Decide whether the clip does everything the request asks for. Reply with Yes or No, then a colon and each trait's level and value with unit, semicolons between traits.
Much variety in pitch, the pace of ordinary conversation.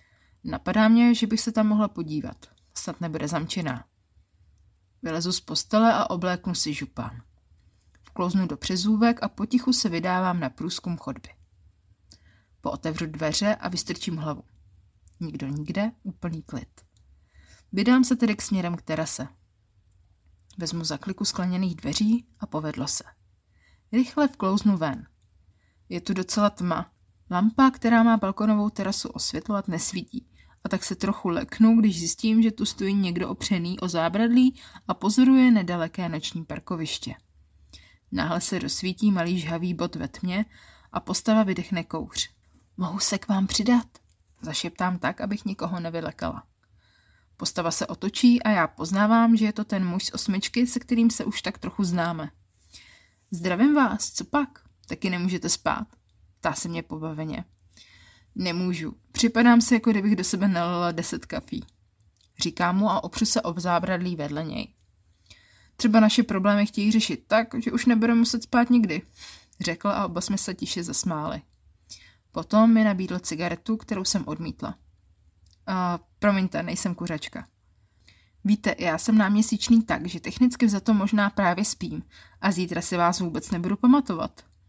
Yes: wide, 8.2 semitones; average, 145 wpm